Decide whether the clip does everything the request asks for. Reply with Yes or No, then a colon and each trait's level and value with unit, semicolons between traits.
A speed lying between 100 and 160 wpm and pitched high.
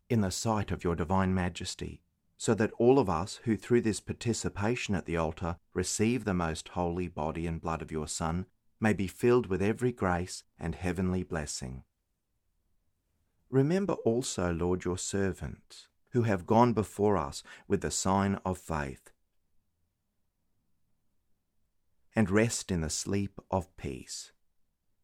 No: average, 145 wpm; very low, 95 Hz